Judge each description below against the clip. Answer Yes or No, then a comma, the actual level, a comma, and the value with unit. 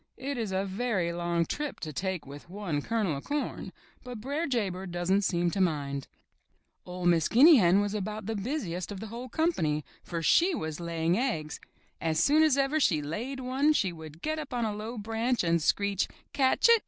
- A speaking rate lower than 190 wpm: No, fast, 205 wpm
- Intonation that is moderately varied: No, wide, 6.8 semitones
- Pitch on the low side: No, high, 200 Hz